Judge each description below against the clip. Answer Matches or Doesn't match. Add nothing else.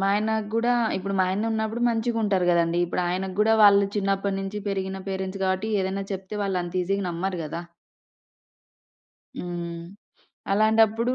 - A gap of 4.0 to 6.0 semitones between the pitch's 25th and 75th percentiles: Doesn't match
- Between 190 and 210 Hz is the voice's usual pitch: Matches